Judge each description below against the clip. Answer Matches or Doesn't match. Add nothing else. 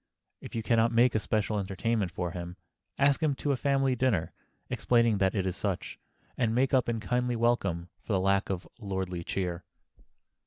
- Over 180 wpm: Matches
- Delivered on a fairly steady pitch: Doesn't match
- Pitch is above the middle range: Doesn't match